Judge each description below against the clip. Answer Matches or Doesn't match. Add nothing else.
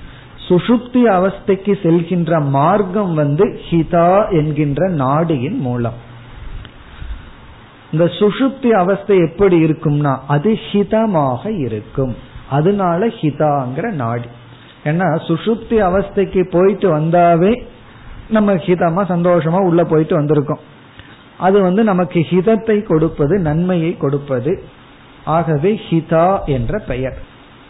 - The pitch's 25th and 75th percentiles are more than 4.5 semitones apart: Matches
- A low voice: Doesn't match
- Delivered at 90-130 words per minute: Doesn't match